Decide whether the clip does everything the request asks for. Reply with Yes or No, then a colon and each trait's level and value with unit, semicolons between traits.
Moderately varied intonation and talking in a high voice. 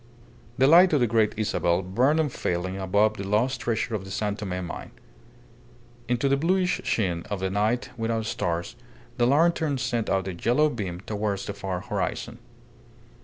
No: average, 4.7 semitones; low, 110 Hz